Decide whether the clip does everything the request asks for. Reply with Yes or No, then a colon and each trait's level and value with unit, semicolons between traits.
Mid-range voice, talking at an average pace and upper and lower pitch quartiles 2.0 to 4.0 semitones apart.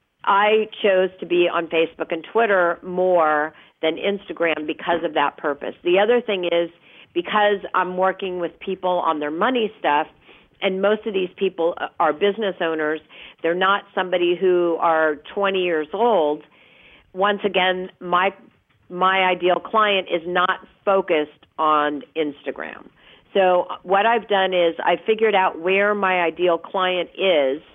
Yes: medium, 180 Hz; average, 145 wpm; average, 2.9 semitones